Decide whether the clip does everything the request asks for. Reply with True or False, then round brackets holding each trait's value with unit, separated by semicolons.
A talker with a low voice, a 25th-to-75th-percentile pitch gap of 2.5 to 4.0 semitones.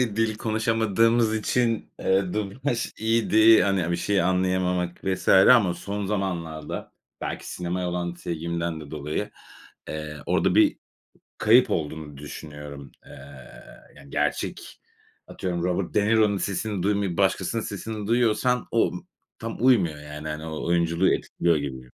False (95 Hz; 4.7 semitones)